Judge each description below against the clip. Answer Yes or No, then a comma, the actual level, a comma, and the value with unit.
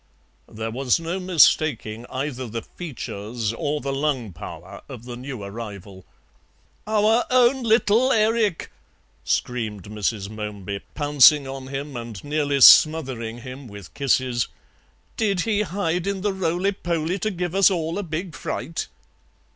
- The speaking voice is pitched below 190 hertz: Yes, medium, 140 Hz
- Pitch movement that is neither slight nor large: No, wide, 7.8 semitones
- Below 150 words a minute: Yes, average, 140 wpm